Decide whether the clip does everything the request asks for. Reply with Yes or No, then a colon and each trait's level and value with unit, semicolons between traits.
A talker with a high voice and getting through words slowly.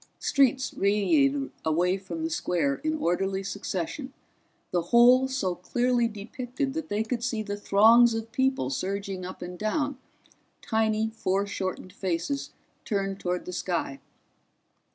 Yes: high, 205 Hz; slow, 130 wpm